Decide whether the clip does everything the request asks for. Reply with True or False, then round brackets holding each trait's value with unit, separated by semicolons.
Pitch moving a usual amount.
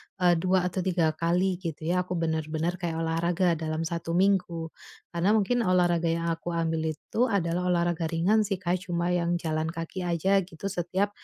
False (1.8 semitones)